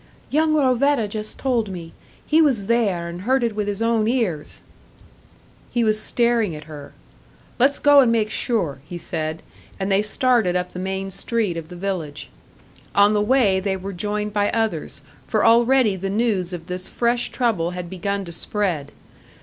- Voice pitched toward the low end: No, high, 205 Hz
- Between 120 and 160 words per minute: No, average, 175 wpm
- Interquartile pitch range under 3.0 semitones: No, average, 4.5 semitones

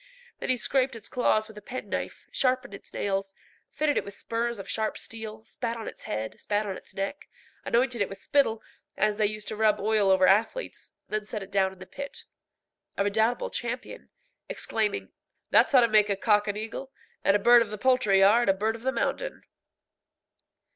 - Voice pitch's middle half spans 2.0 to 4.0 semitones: Yes, average, 3.0 semitones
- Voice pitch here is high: Yes, high, 215 Hz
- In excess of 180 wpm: Yes, average, 200 wpm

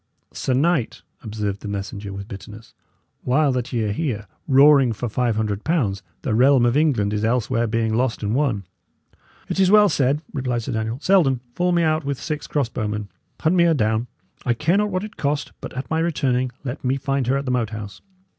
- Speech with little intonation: No, average, 5.2 semitones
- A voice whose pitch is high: No, low, 125 Hz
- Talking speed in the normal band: No, fast, 210 wpm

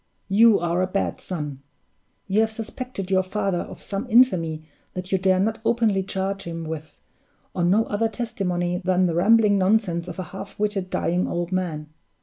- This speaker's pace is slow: No, average, 175 wpm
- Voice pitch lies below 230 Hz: Yes, high, 190 Hz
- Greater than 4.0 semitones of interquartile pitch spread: No, average, 3.2 semitones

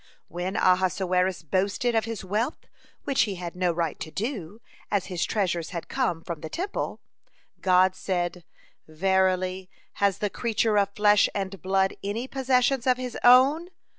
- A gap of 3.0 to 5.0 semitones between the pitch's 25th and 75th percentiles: Yes, average, 4.1 semitones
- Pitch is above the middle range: Yes, high, 195 Hz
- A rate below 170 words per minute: Yes, average, 160 wpm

